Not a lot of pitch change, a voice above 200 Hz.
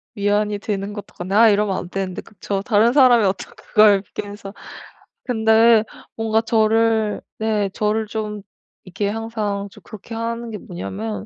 Yes: narrow, 1.9 semitones; high, 210 Hz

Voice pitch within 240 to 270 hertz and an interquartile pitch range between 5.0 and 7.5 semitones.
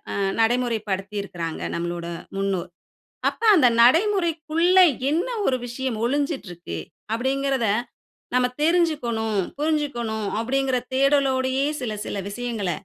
Yes: very high, 250 Hz; wide, 5.4 semitones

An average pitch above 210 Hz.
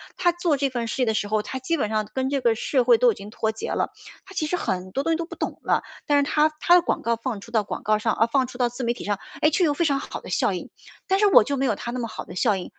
Yes: very high, 250 Hz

